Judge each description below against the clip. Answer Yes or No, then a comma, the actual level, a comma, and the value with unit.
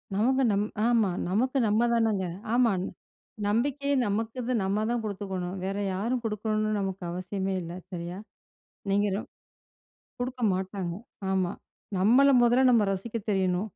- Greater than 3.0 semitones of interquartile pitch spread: Yes, average, 3.8 semitones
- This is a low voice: No, high, 210 Hz